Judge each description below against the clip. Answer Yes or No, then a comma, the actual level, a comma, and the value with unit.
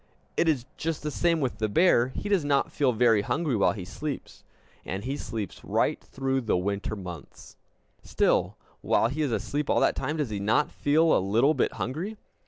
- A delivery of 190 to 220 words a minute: Yes, average, 195 wpm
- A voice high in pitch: No, low, 130 Hz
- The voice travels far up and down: Yes, wide, 5.9 semitones